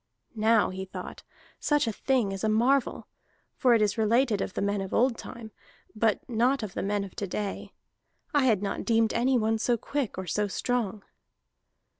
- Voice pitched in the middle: No, high, 220 Hz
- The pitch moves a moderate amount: Yes, average, 3.1 semitones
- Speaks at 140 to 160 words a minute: No, average, 185 wpm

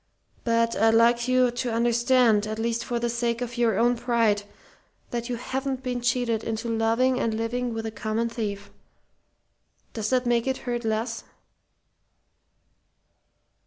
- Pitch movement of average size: No, narrow, 1.5 semitones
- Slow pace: No, average, 150 wpm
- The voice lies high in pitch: Yes, high, 235 Hz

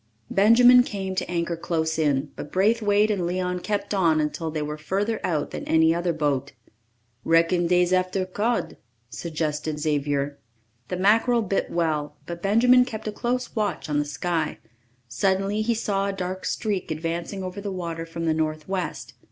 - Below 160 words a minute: No, average, 165 wpm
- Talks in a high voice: No, medium, 180 Hz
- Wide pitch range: No, average, 4.2 semitones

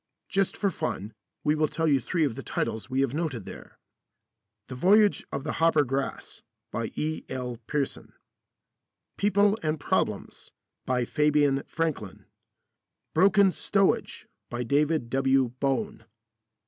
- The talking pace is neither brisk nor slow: No, slow, 125 wpm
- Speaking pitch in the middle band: Yes, medium, 150 Hz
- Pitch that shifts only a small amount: No, average, 4.1 semitones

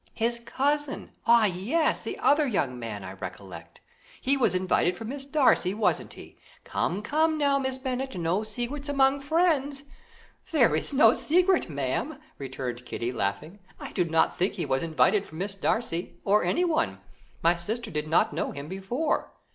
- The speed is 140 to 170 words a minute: Yes, average, 165 wpm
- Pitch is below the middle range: No, high, 220 Hz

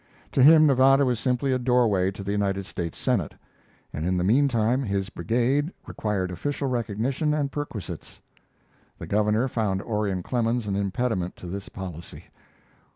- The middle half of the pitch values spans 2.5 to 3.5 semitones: No, average, 4.9 semitones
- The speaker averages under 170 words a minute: Yes, average, 155 wpm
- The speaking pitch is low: Yes, low, 110 Hz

